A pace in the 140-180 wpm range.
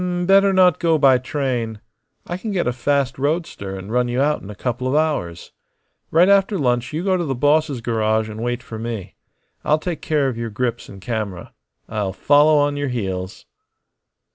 No: average, 190 wpm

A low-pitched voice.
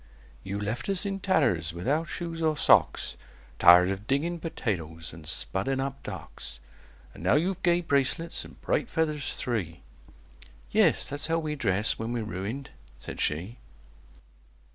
Yes: low, 125 Hz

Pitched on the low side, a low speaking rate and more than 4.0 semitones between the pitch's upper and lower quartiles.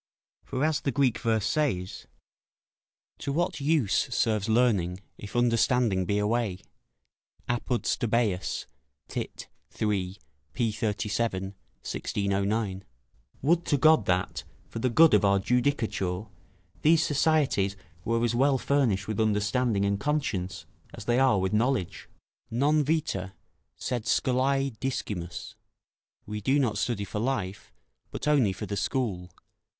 Yes: low, 115 Hz; slow, 125 wpm; average, 5.0 semitones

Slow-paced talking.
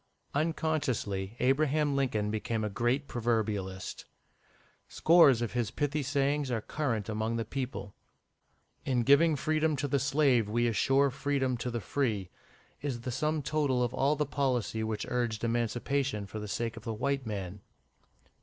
No: average, 155 wpm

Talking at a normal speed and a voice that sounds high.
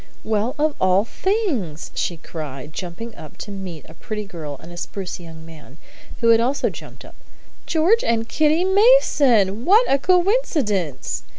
Yes: average, 160 wpm; high, 215 Hz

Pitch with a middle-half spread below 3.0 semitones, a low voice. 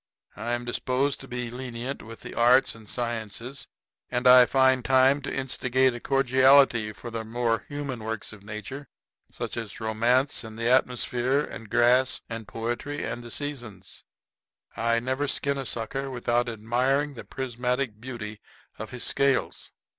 Yes: narrow, 2.5 semitones; low, 125 Hz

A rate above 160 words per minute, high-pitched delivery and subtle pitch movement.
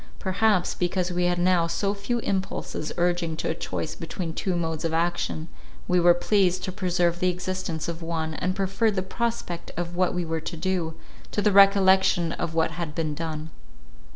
No: average, 185 wpm; medium, 175 Hz; narrow, 2.3 semitones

